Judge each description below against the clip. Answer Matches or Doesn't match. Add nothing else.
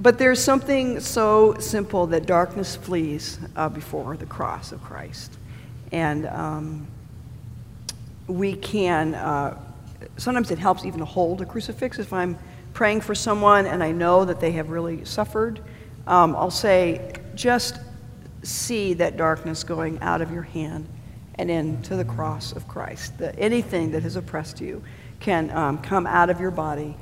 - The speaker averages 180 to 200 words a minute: Doesn't match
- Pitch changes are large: Doesn't match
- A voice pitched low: Doesn't match